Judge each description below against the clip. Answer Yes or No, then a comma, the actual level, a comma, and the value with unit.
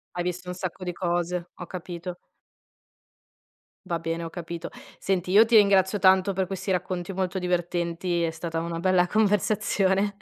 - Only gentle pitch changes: Yes, narrow, 1.8 semitones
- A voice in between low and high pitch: Yes, medium, 180 Hz